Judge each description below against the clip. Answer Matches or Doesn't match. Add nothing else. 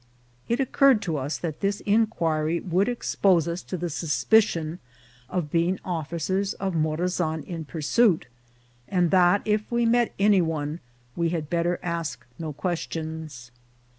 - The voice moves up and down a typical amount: Matches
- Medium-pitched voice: Matches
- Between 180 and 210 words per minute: Doesn't match